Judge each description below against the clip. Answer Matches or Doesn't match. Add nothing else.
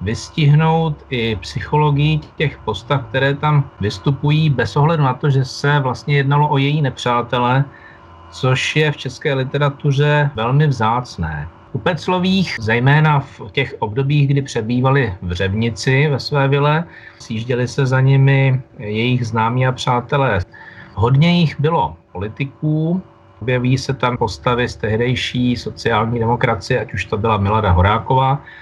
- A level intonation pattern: Doesn't match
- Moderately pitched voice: Doesn't match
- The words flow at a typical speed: Matches